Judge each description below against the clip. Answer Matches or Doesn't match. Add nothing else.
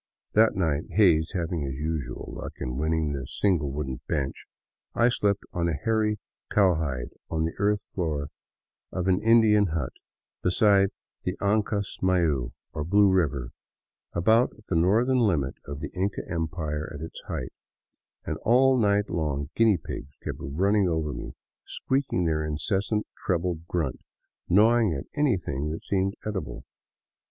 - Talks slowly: Doesn't match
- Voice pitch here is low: Matches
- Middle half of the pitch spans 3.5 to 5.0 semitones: Doesn't match